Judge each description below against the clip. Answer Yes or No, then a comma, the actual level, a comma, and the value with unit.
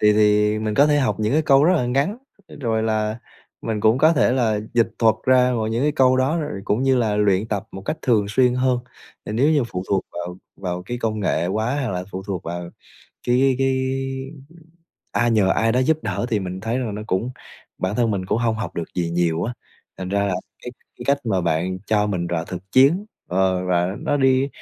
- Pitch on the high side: No, low, 110 Hz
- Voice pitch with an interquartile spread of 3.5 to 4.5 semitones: No, average, 5.3 semitones